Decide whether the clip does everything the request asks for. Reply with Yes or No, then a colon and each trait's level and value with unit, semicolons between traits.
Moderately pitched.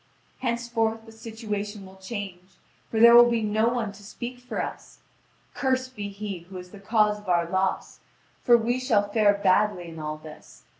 No: high, 210 Hz